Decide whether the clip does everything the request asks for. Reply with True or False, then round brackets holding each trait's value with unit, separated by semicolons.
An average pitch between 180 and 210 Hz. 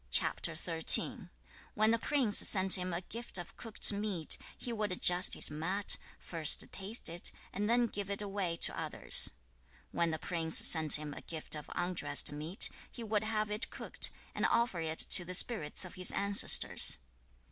True (190 Hz)